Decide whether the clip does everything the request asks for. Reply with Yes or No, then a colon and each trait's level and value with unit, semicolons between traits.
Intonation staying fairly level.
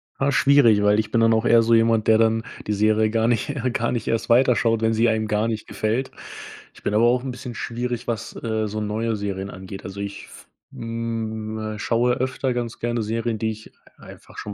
Yes: narrow, 1.5 semitones